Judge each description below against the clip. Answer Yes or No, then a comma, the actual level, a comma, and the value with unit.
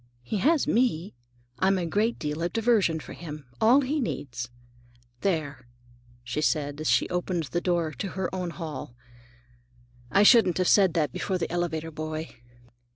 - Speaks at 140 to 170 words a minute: Yes, average, 160 wpm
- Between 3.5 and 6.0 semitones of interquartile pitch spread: Yes, average, 4.2 semitones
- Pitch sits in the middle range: Yes, medium, 170 Hz